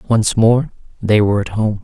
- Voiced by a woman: No, male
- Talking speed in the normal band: Yes, average, 195 wpm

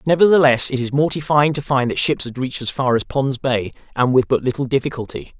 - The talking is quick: Yes, fast, 225 wpm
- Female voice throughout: No, male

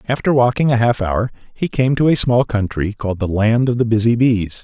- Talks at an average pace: No, fast, 235 wpm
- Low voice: Yes, low, 115 Hz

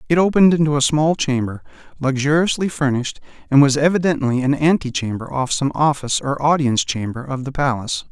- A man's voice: Yes, male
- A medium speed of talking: Yes, average, 170 wpm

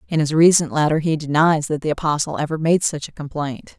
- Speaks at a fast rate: Yes, fast, 220 wpm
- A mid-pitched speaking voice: Yes, medium, 155 Hz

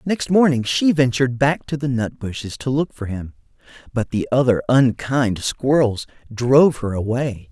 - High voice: No, low, 125 Hz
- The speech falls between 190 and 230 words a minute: No, average, 170 wpm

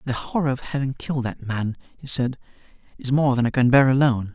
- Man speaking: Yes, male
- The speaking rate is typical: No, fast, 220 wpm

